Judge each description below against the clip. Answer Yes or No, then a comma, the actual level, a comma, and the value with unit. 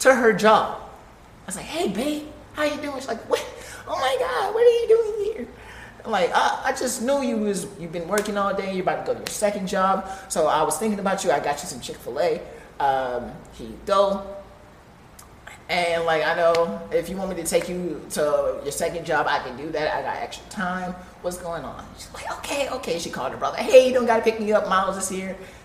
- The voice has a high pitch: Yes, high, 195 Hz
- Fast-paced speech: Yes, fast, 240 wpm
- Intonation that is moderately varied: No, wide, 6.8 semitones